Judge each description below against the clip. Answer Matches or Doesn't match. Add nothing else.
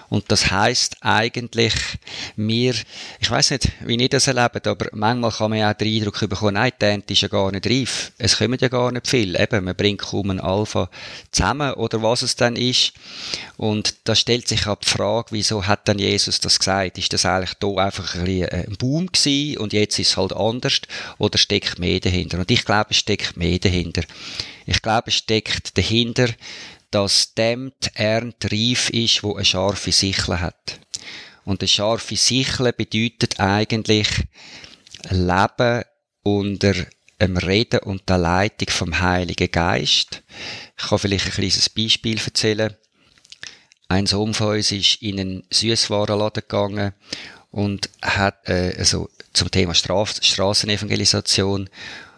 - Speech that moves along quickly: Doesn't match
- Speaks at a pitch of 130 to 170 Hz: Doesn't match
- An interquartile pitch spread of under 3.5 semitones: Matches